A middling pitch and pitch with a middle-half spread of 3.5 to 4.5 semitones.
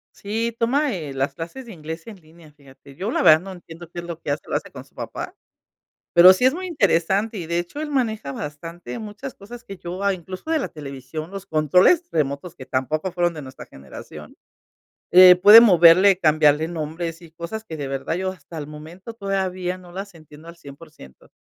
Yes: medium, 175 Hz; average, 4.2 semitones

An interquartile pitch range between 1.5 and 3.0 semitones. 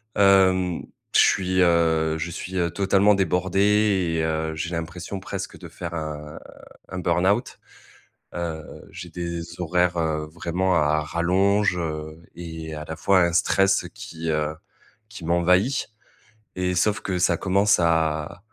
Yes: narrow, 2.6 semitones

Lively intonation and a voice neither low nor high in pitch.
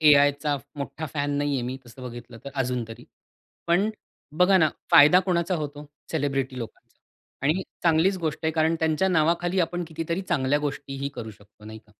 No: average, 4.0 semitones; medium, 145 Hz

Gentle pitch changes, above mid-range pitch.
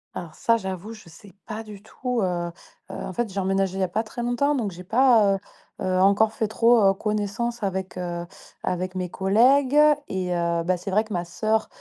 No: average, 3.4 semitones; high, 195 Hz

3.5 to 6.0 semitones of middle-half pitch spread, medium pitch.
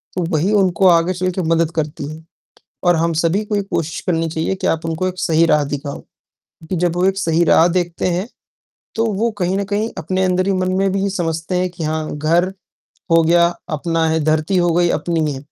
No: narrow, 2.4 semitones; medium, 170 Hz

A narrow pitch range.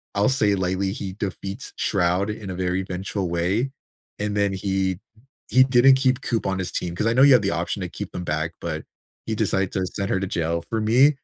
No: average, 3.3 semitones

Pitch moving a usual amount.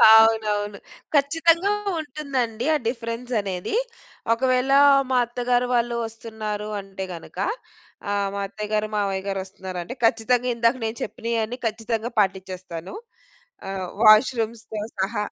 Yes: average, 3.2 semitones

